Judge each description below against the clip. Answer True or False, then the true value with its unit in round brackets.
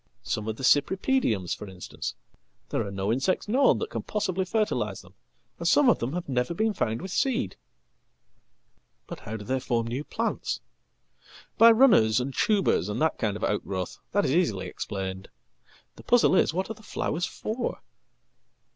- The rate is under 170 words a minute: True (155 wpm)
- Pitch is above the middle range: False (135 Hz)